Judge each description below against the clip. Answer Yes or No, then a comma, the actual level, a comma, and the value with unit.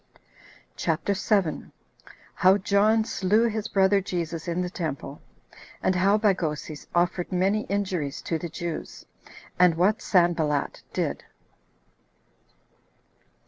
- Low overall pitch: No, medium, 185 Hz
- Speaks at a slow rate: Yes, slow, 105 wpm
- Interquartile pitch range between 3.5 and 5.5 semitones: No, average, 3.1 semitones